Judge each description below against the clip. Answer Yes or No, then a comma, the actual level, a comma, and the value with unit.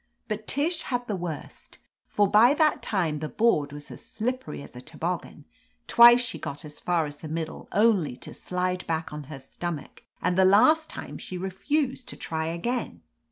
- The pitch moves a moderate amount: No, wide, 7.1 semitones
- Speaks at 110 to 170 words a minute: No, average, 190 wpm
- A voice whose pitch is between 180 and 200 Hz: Yes, medium, 185 Hz